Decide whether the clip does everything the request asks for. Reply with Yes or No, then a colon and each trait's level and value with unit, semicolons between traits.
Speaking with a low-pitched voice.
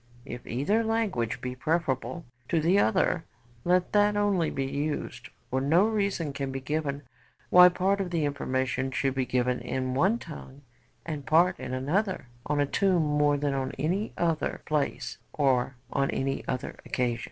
No: medium, 145 Hz